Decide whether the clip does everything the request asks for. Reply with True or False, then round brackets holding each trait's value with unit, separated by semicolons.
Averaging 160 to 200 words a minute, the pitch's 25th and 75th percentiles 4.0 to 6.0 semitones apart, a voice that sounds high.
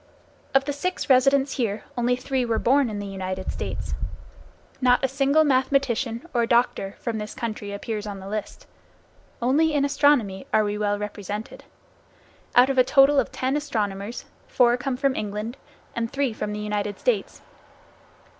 True (165 wpm; 4.5 semitones; 240 Hz)